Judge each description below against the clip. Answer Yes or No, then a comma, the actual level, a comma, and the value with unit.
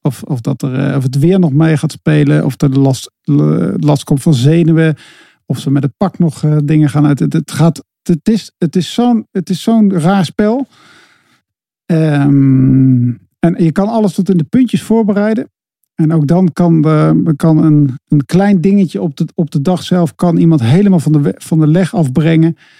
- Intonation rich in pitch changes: No, average, 3.7 semitones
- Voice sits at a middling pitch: Yes, medium, 160 Hz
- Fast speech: Yes, fast, 205 wpm